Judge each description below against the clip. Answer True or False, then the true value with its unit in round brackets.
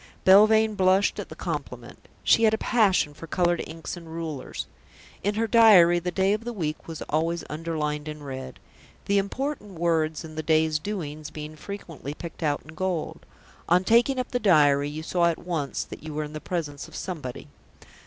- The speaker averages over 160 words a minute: True (190 wpm)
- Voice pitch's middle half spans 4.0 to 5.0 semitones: True (4.4 semitones)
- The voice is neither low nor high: True (165 Hz)